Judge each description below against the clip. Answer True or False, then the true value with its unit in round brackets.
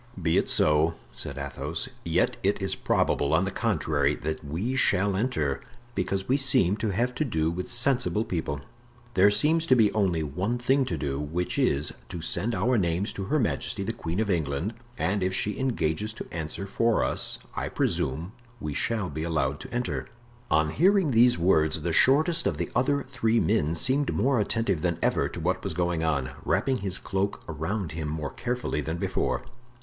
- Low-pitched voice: True (95 Hz)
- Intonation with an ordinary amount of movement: False (7.2 semitones)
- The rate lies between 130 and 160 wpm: False (190 wpm)